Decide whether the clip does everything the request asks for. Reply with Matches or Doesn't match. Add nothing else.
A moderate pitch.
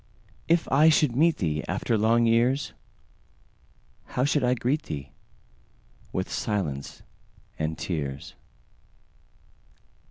Doesn't match